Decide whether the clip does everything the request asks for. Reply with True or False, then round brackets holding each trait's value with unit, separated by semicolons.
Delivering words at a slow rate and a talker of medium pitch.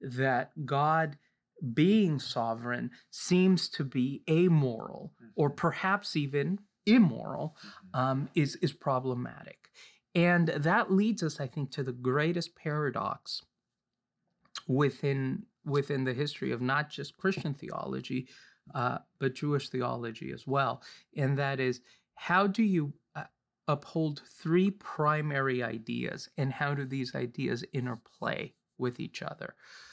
True (120 wpm; 145 Hz)